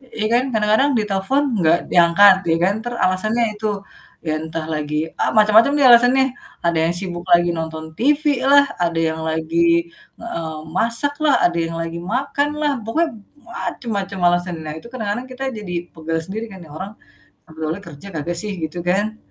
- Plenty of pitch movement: Yes, wide, 5.9 semitones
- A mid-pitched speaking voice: No, high, 195 Hz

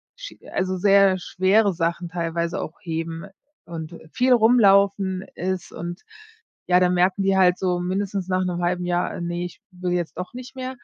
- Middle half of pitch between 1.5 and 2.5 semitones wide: Yes, narrow, 2.0 semitones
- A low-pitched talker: No, medium, 180 Hz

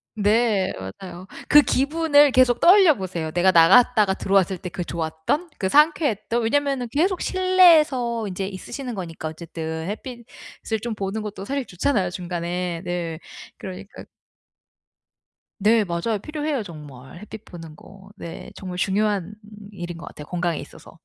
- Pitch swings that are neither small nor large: No, wide, 6.1 semitones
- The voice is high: Yes, high, 200 Hz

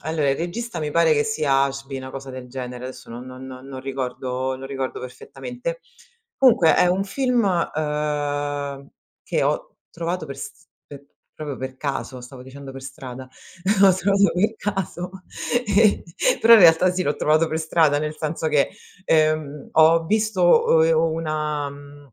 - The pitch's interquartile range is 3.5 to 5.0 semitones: Yes, average, 4.1 semitones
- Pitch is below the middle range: No, medium, 150 Hz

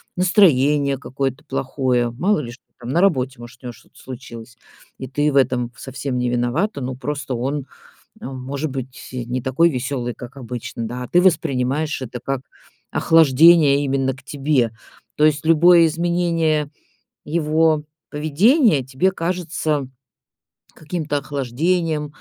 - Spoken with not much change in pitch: No, average, 3.8 semitones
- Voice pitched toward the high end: No, medium, 140 Hz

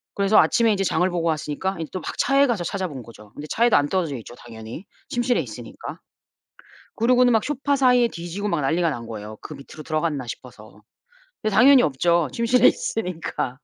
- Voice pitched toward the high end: No, medium, 175 Hz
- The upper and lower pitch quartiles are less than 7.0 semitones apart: No, wide, 8.6 semitones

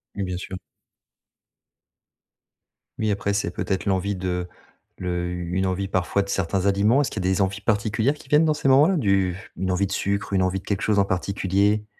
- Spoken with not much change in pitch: Yes, narrow, 2.0 semitones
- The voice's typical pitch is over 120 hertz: No, low, 100 Hz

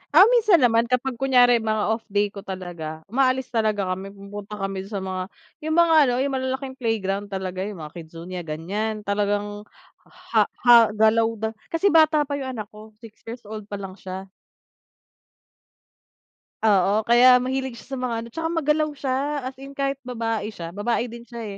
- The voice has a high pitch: Yes, high, 220 Hz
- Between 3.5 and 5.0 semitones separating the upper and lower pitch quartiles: Yes, average, 4.5 semitones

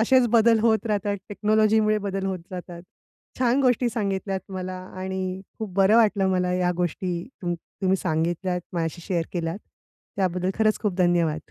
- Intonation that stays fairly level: No, average, 3.1 semitones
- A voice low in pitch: No, high, 190 Hz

